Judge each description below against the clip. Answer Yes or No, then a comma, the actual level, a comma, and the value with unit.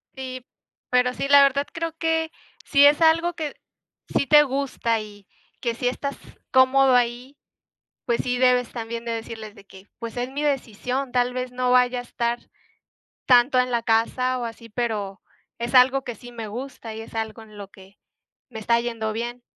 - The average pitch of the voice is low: No, high, 245 Hz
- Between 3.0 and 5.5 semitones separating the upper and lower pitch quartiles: No, narrow, 2.4 semitones